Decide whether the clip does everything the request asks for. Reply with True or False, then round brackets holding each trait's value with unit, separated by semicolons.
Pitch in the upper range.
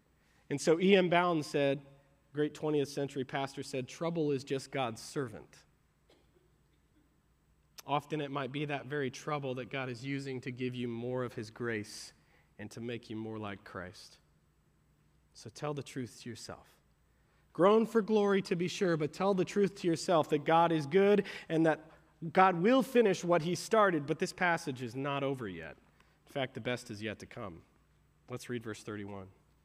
False (140 Hz)